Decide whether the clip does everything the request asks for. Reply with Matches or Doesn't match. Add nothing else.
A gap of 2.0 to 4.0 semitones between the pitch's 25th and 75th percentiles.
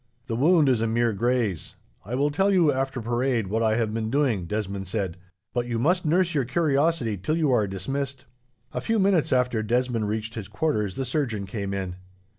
Doesn't match